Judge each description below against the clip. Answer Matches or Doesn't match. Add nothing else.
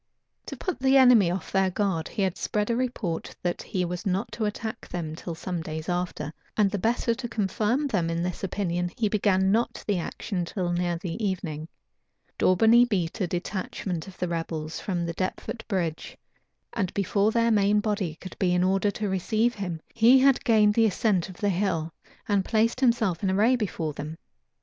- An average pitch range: Matches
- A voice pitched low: Doesn't match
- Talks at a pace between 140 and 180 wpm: Doesn't match